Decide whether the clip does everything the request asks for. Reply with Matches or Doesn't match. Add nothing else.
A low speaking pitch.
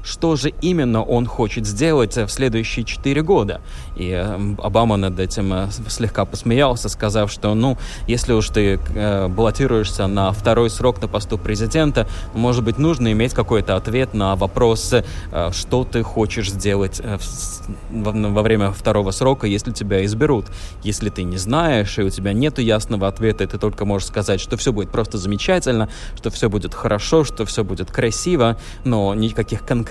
Matches